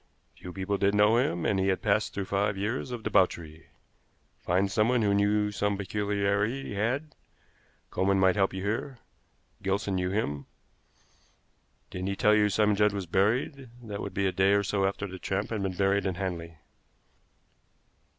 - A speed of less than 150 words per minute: No, average, 180 wpm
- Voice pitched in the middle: No, low, 100 Hz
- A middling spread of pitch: No, narrow, 1.7 semitones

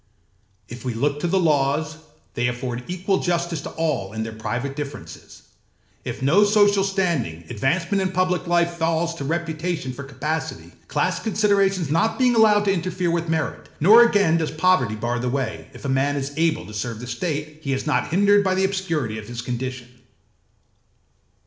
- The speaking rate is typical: Yes, average, 180 wpm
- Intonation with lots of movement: Yes, wide, 6.1 semitones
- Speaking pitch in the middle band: Yes, medium, 160 Hz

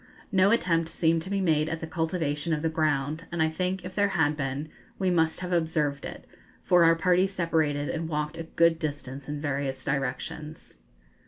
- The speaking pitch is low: No, medium, 160 Hz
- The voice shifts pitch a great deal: No, narrow, 2.6 semitones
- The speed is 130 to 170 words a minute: No, average, 190 wpm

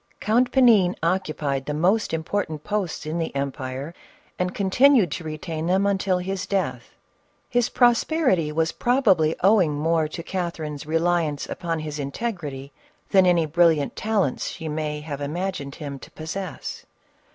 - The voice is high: No, medium, 170 Hz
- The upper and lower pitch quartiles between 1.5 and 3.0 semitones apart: No, average, 4.2 semitones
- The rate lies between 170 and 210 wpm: No, average, 145 wpm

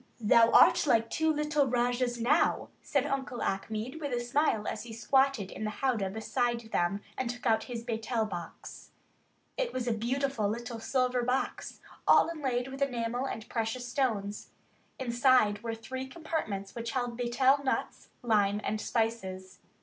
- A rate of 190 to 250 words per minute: No, average, 155 wpm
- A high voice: Yes, high, 240 Hz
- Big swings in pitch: No, average, 2.9 semitones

